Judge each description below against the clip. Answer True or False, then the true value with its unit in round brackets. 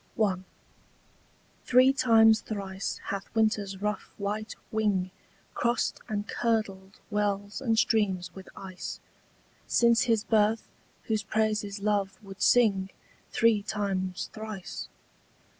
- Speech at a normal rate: False (105 wpm)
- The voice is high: True (210 Hz)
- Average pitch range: False (2.1 semitones)